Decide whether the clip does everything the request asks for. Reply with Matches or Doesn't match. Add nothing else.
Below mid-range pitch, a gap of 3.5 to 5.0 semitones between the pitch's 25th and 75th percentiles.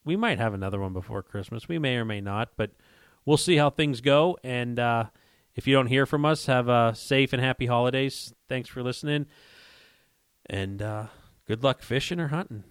Matches